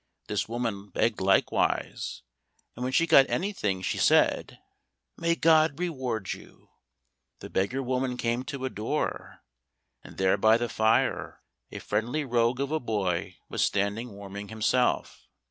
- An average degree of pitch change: Yes, average, 4.6 semitones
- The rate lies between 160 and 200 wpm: No, average, 145 wpm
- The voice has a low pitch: Yes, low, 120 Hz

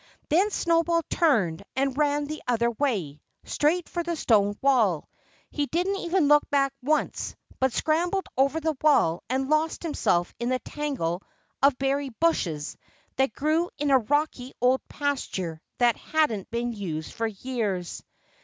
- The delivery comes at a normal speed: Yes, average, 150 wpm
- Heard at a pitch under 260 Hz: No, very high, 275 Hz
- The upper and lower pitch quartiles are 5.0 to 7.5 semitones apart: Yes, wide, 5.4 semitones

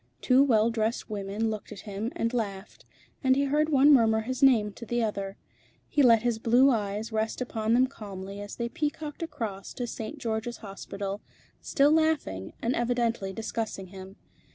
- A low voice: No, high, 225 Hz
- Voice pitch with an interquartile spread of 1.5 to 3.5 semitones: No, average, 3.9 semitones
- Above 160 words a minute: Yes, average, 175 wpm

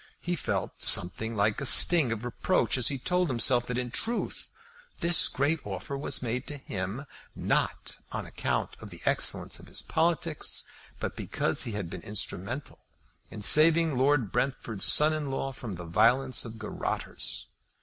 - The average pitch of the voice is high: No, low, 125 Hz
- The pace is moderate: Yes, average, 165 wpm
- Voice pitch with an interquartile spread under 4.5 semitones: No, wide, 5.5 semitones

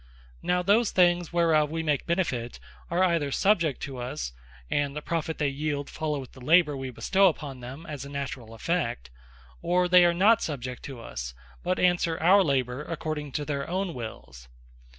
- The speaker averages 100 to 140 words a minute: No, average, 175 wpm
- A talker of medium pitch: Yes, medium, 150 Hz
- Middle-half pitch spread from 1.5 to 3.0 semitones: No, average, 4.8 semitones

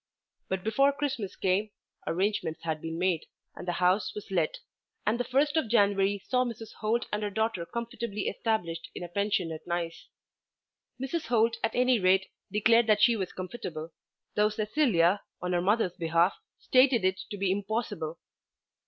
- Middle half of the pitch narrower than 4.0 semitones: No, average, 4.3 semitones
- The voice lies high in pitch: Yes, high, 205 Hz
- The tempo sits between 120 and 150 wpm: No, average, 165 wpm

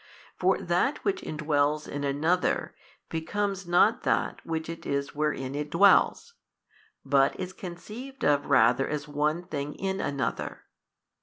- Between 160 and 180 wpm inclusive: No, slow, 135 wpm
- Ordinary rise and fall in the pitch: Yes, average, 4.4 semitones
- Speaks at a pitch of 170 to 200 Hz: No, medium, 155 Hz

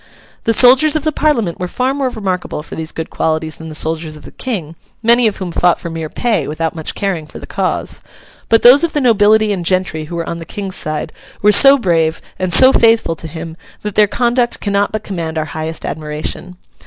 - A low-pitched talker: No, medium, 185 Hz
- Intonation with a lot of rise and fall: Yes, wide, 6.1 semitones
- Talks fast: Yes, fast, 220 wpm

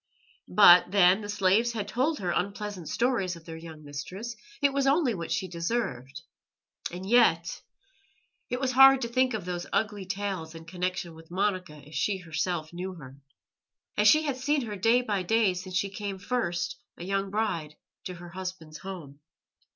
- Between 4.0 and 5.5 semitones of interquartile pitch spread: Yes, average, 4.6 semitones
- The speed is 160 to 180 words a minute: Yes, average, 175 wpm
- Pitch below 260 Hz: Yes, high, 190 Hz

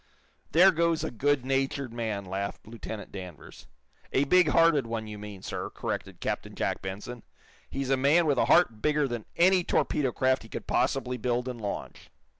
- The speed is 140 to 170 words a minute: No, average, 180 wpm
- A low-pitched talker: Yes, low, 130 Hz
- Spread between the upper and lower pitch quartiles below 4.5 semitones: No, average, 4.9 semitones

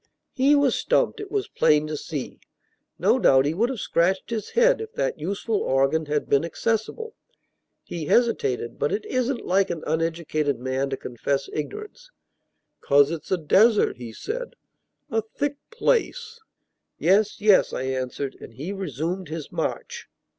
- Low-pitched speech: No, medium, 180 Hz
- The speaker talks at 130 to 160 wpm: Yes, average, 155 wpm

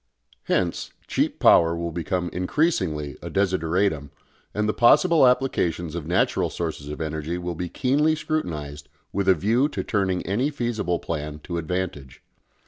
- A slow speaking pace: No, average, 145 wpm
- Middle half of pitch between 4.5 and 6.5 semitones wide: Yes, average, 5.0 semitones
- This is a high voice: No, very low, 90 Hz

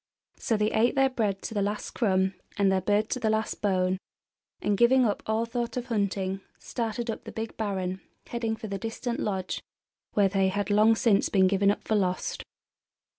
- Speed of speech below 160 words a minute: No, average, 195 wpm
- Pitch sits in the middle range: No, high, 210 Hz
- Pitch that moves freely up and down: No, average, 2.7 semitones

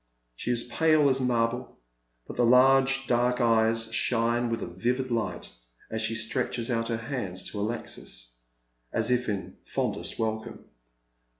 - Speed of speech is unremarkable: Yes, average, 145 wpm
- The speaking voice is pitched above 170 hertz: No, low, 115 Hz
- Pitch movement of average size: No, narrow, 2.0 semitones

